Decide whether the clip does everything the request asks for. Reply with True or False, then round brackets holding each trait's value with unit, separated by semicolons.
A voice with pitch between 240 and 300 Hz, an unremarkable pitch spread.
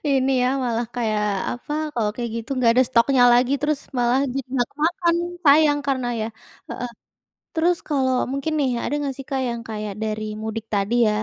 True (255 Hz; 3.3 semitones)